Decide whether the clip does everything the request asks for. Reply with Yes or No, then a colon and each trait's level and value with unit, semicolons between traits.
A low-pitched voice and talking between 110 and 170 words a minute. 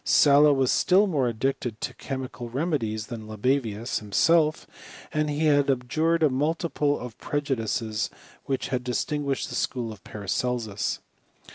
Yes: low, 130 Hz; average, 140 wpm